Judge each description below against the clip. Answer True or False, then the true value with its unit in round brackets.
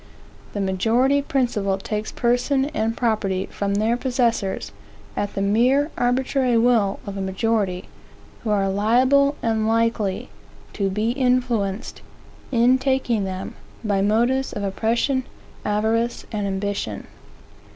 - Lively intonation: False (3.8 semitones)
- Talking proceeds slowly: True (120 wpm)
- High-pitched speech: True (225 Hz)